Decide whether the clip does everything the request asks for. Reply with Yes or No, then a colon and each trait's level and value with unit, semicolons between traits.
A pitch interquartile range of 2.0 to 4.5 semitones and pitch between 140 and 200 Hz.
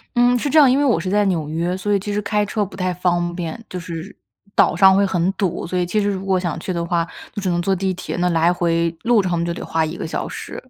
Yes: average, 2.8 semitones; medium, 185 Hz